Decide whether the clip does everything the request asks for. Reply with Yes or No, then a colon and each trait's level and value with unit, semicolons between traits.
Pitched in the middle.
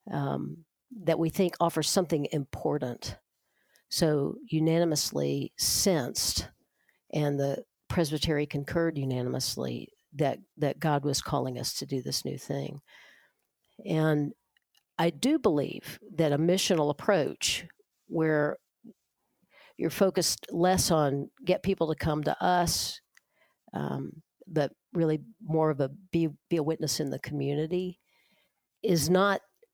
Yes: medium, 155 Hz